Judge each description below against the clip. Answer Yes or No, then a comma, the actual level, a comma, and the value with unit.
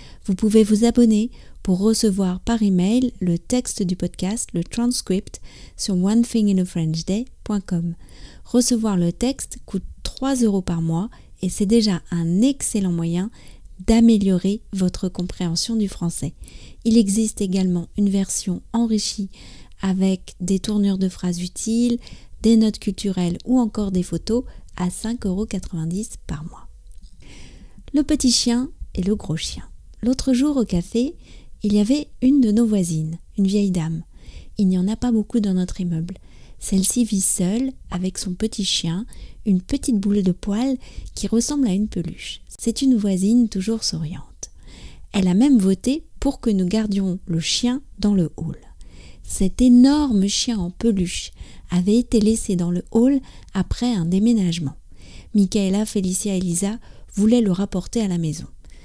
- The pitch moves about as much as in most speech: Yes, average, 4.1 semitones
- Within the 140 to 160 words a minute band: Yes, average, 150 wpm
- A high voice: Yes, high, 200 Hz